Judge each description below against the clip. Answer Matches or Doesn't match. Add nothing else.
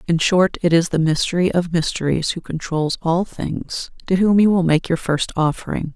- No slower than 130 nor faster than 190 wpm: Doesn't match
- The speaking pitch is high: Doesn't match